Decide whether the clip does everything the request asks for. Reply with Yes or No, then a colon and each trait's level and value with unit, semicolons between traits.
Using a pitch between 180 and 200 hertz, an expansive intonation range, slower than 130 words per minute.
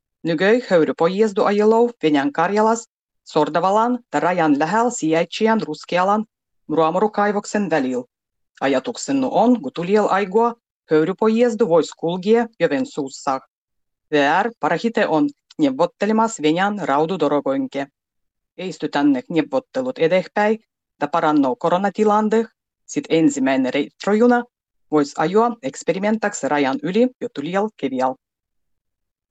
Yes: high, 190 Hz; wide, 7.1 semitones; average, 100 wpm